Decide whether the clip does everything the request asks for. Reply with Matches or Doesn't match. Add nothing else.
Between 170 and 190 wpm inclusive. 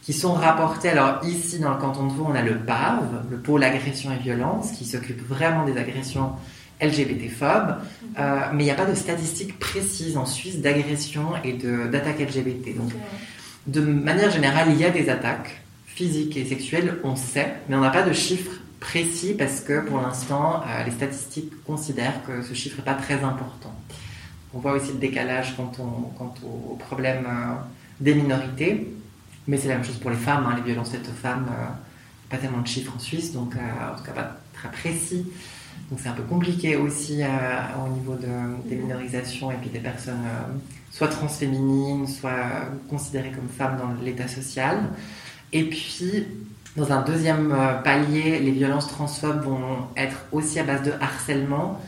Matches